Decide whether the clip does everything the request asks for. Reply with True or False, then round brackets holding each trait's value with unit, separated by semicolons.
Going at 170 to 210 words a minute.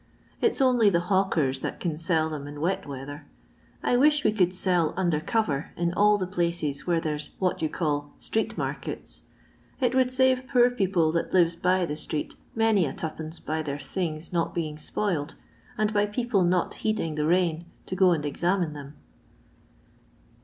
True (185 wpm)